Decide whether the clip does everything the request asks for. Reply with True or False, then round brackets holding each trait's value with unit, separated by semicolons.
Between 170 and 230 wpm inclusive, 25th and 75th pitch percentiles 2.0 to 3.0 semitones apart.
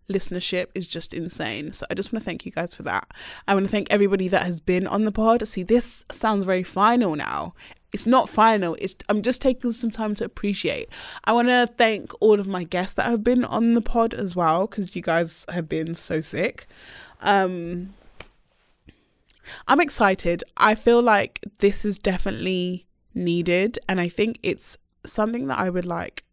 False (190 wpm; 4.0 semitones)